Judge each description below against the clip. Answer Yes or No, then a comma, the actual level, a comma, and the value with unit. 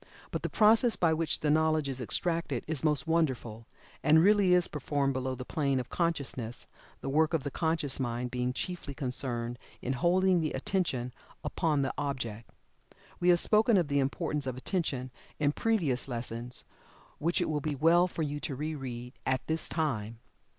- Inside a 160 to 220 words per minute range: Yes, average, 180 wpm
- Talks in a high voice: No, medium, 145 Hz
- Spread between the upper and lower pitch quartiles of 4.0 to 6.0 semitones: Yes, average, 4.4 semitones